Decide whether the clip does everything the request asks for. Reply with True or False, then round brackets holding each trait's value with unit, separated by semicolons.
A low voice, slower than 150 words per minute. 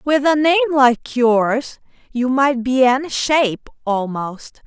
False (260 Hz; 140 wpm)